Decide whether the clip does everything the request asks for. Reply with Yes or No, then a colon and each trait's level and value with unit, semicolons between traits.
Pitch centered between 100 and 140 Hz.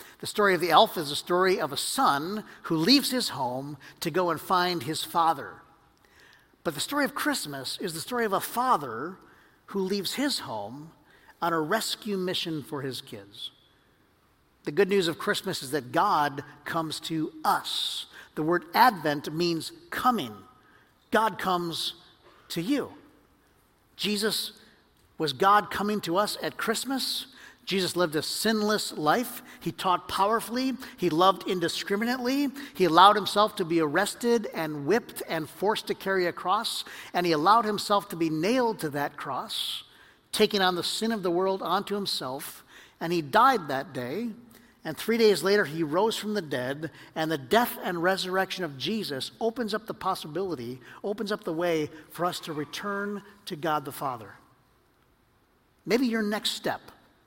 No: high, 190 Hz